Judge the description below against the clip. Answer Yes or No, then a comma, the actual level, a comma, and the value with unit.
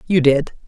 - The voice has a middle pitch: Yes, medium, 155 Hz